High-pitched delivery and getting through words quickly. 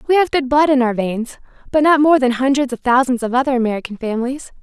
Yes: very high, 260 Hz; fast, 235 wpm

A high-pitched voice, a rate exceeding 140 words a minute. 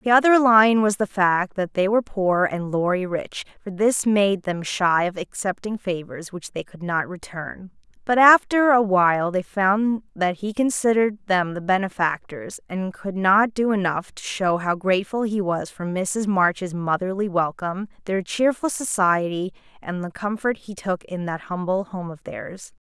Yes: high, 195 Hz; average, 180 wpm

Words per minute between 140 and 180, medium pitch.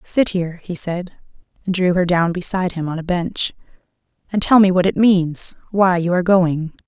No: average, 200 wpm; medium, 180 Hz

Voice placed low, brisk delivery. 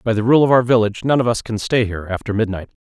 Yes: low, 115 Hz; fast, 295 wpm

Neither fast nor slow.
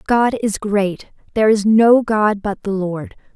Yes: average, 180 wpm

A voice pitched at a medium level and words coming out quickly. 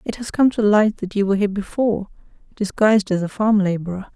No: high, 205 Hz; fast, 215 wpm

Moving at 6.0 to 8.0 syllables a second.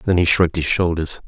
Yes: 6.4 syllables/s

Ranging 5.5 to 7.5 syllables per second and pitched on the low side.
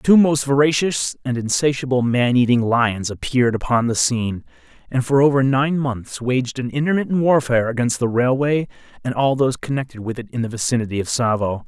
Yes: 5.6 syllables/s; low, 125 Hz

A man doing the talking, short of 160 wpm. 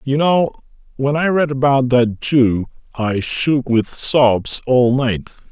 Yes: male; average, 150 wpm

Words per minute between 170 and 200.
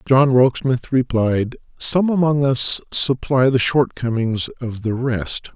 No: average, 140 wpm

